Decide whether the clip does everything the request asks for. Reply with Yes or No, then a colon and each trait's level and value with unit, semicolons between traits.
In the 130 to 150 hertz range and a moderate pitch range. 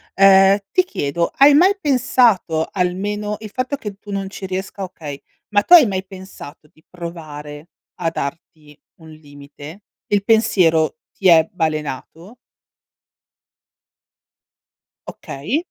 No: medium, 185 Hz; average, 4.8 semitones